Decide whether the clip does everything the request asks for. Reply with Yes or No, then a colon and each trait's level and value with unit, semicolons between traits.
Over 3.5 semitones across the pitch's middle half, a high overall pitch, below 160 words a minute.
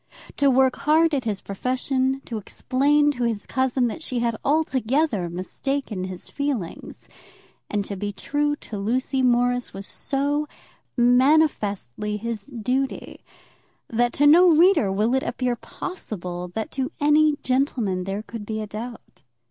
Yes: average, 5.1 semitones; high, 245 Hz; average, 145 wpm